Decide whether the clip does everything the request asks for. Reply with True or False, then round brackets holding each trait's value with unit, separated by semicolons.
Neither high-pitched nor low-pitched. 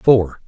False (105 Hz)